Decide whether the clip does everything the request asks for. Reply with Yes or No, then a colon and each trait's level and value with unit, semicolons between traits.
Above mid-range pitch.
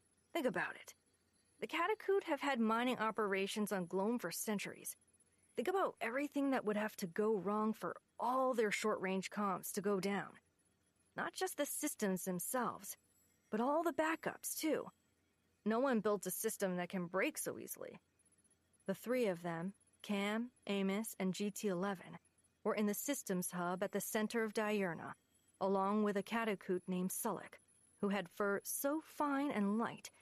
Yes: high, 210 Hz